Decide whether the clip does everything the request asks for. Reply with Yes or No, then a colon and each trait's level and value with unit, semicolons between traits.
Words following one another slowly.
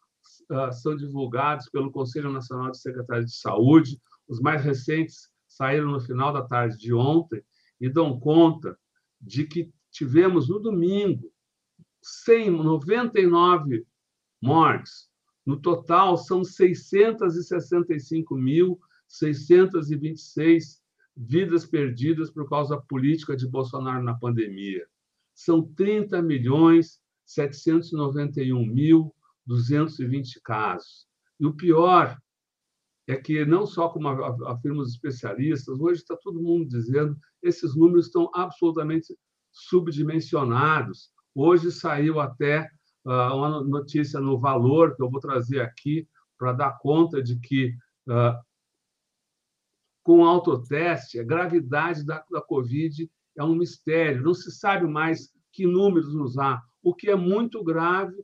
Yes: slow, 115 wpm